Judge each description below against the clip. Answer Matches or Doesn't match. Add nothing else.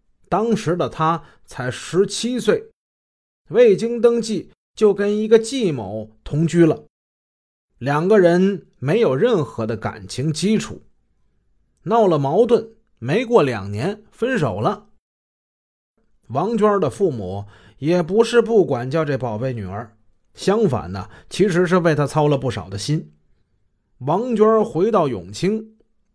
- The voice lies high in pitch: Doesn't match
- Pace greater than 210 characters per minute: Doesn't match